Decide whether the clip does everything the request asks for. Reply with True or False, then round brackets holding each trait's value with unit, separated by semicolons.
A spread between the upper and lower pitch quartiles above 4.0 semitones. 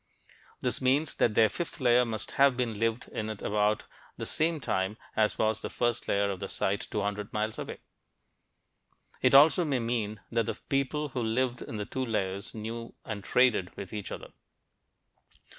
False (3.5 semitones)